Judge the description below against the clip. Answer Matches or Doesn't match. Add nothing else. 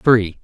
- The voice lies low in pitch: Matches